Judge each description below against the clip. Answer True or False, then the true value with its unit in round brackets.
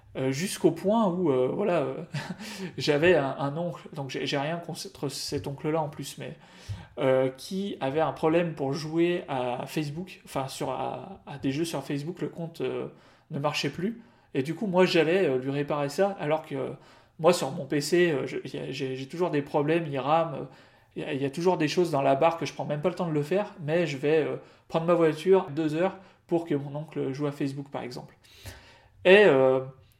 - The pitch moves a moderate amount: True (4.2 semitones)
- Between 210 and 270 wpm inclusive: True (220 wpm)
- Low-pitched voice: False (150 Hz)